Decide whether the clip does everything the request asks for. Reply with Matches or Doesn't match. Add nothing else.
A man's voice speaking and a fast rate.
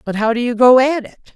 Doesn't match